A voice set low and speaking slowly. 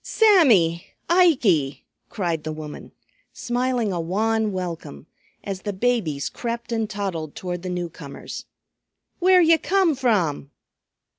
No: high, 200 Hz; slow, 120 wpm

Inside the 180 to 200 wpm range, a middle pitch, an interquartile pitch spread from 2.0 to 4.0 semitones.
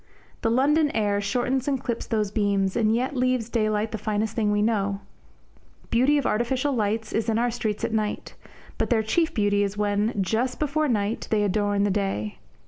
No: average, 190 wpm; high, 220 Hz; average, 3.0 semitones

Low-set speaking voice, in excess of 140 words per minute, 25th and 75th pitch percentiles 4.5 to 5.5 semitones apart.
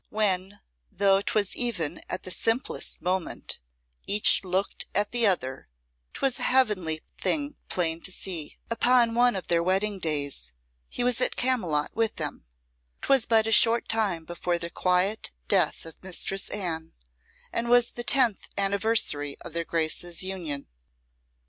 No: high, 195 Hz; average, 150 wpm; average, 5.0 semitones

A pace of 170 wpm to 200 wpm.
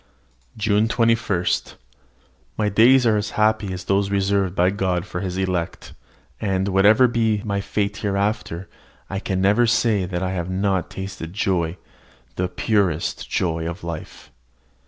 No: average, 145 wpm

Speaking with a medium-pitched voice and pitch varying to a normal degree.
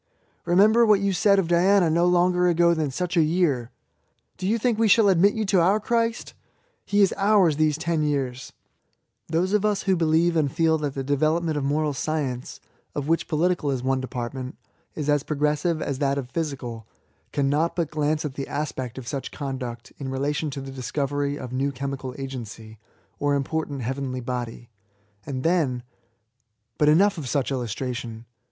Yes: medium, 150 Hz; average, 4.6 semitones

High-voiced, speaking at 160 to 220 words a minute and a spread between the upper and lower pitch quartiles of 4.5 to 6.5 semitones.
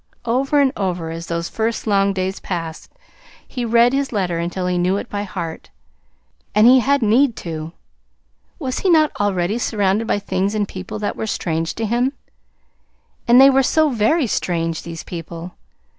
Yes: high, 205 Hz; average, 175 wpm; wide, 5.6 semitones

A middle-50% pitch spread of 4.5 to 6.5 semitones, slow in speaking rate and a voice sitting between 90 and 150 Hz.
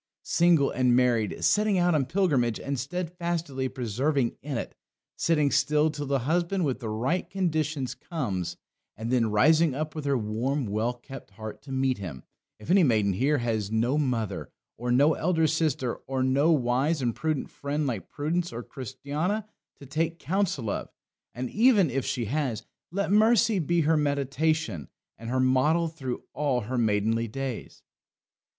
No: average, 4.8 semitones; average, 165 wpm; medium, 140 Hz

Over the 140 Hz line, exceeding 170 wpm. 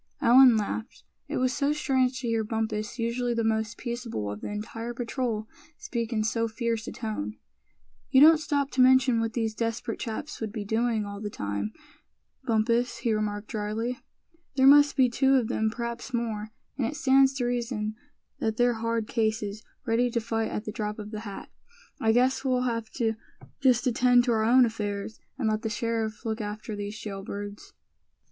Yes: high, 230 Hz; average, 185 wpm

